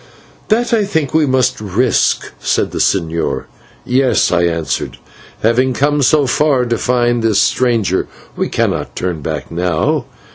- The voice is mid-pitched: No, low, 125 Hz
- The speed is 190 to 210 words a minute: No, average, 160 wpm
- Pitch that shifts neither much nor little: No, wide, 7.0 semitones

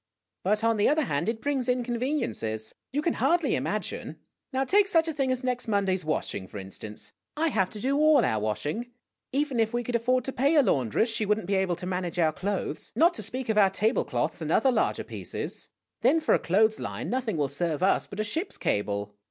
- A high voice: Yes, high, 220 Hz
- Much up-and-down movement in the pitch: Yes, wide, 6.9 semitones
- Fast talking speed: Yes, fast, 235 wpm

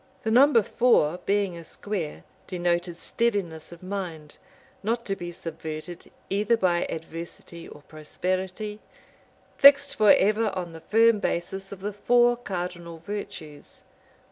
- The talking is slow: Yes, slow, 125 wpm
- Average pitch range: Yes, average, 4.0 semitones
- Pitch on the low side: No, medium, 185 Hz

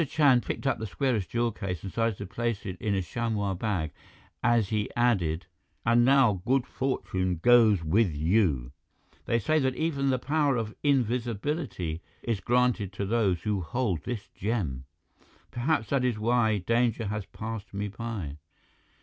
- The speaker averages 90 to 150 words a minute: No, average, 160 wpm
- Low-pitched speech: Yes, low, 110 Hz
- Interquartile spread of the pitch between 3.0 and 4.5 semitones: Yes, average, 4.2 semitones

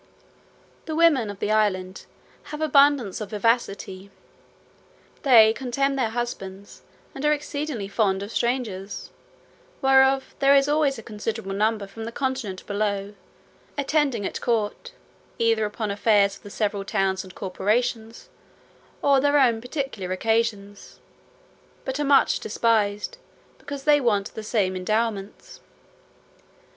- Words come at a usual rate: No, slow, 130 wpm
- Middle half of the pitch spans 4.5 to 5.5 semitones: Yes, average, 4.9 semitones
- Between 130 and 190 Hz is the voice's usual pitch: No, high, 225 Hz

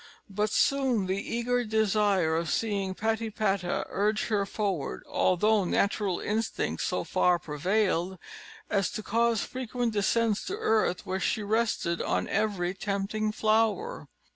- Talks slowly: Yes, slow, 130 wpm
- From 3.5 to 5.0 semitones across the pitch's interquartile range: No, average, 2.7 semitones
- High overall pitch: Yes, high, 210 Hz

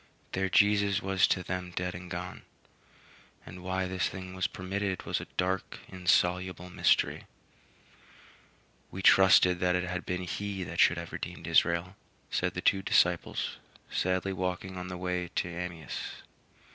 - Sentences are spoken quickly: No, average, 150 wpm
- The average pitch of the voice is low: Yes, very low, 90 Hz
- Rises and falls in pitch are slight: Yes, narrow, 0.9 semitones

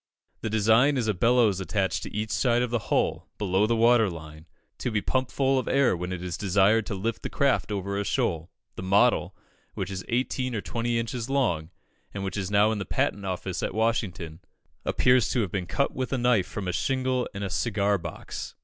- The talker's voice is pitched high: No, low, 105 Hz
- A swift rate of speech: Yes, fast, 215 wpm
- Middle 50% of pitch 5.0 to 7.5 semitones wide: No, average, 4.2 semitones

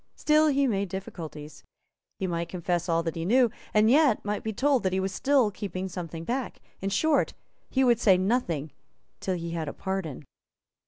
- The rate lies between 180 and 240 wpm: Yes, average, 190 wpm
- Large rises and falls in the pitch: Yes, wide, 6.1 semitones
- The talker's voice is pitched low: No, high, 190 Hz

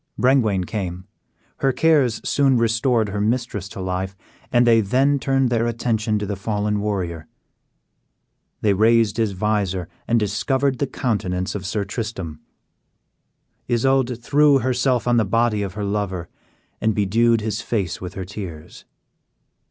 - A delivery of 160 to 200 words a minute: No, average, 145 wpm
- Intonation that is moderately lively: Yes, average, 3.7 semitones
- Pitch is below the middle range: Yes, low, 110 Hz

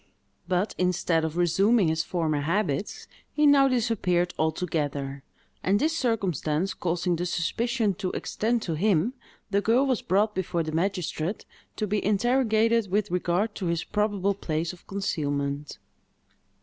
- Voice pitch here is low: No, medium, 185 Hz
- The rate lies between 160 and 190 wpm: No, average, 140 wpm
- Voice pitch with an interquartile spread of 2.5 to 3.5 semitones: No, average, 4.6 semitones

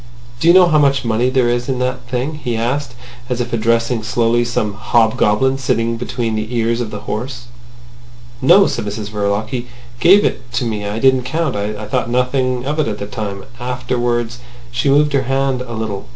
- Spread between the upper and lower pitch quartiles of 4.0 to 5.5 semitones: No, average, 2.7 semitones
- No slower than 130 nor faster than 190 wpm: No, average, 200 wpm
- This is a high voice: No, low, 120 Hz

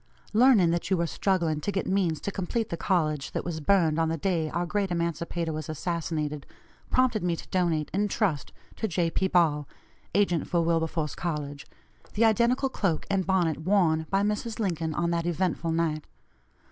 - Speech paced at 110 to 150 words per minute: No, average, 180 wpm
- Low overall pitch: No, medium, 170 Hz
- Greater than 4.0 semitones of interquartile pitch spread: No, average, 3.4 semitones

